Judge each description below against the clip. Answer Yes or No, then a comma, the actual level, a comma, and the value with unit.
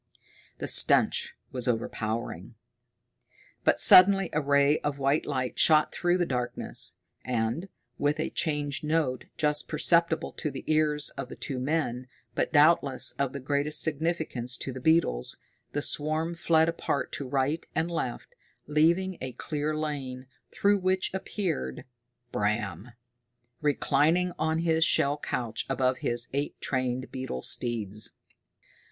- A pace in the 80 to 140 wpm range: Yes, slow, 135 wpm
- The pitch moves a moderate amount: Yes, average, 4.0 semitones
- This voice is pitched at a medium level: Yes, medium, 145 Hz